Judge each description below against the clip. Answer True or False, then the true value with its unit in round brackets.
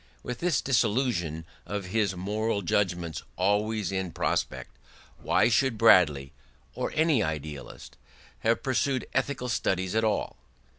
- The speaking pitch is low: True (105 Hz)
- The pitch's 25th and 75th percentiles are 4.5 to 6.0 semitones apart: True (4.8 semitones)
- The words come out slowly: True (120 wpm)